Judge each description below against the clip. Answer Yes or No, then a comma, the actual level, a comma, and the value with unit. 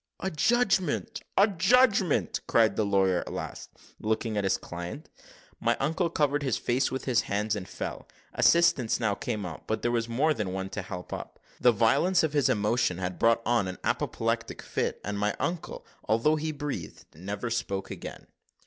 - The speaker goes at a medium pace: Yes, average, 180 wpm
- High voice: No, low, 115 Hz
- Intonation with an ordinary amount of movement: No, wide, 6.9 semitones